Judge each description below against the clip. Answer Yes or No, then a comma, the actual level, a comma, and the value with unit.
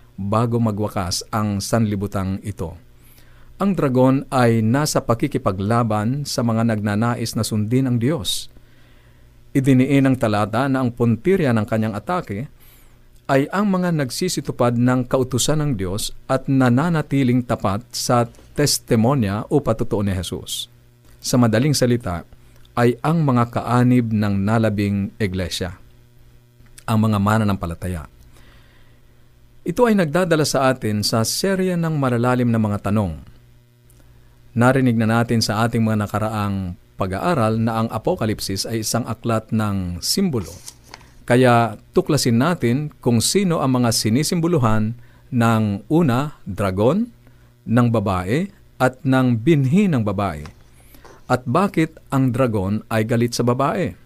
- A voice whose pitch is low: Yes, low, 120 Hz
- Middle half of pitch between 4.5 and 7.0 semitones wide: No, average, 3.3 semitones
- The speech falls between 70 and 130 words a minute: Yes, average, 125 wpm